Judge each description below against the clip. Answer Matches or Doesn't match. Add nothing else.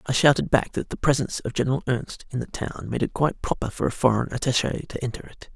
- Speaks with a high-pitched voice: Doesn't match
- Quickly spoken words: Matches